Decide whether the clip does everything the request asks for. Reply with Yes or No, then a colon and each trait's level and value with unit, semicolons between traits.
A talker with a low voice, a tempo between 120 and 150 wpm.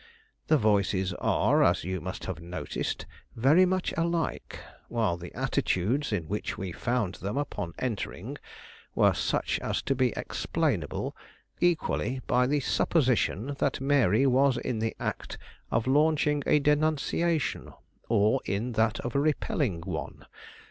Yes: low, 125 Hz; slow, 135 wpm